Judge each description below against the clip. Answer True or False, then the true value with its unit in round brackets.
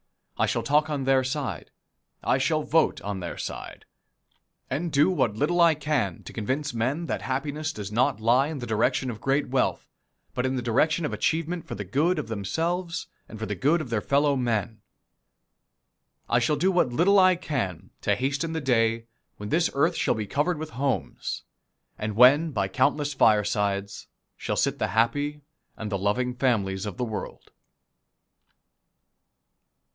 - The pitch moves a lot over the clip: True (5.7 semitones)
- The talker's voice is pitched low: True (130 Hz)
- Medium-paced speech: True (170 wpm)